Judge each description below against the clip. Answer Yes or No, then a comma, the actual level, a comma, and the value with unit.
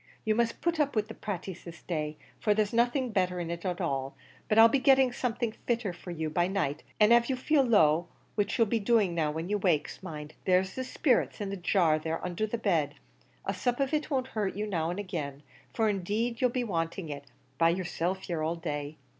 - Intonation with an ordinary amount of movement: No, wide, 5.8 semitones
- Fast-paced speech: Yes, fast, 220 wpm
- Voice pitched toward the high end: Yes, high, 195 Hz